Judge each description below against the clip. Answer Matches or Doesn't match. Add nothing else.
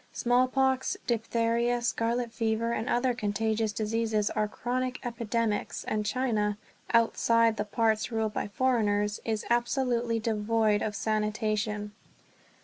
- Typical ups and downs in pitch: Doesn't match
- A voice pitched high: Matches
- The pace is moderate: Doesn't match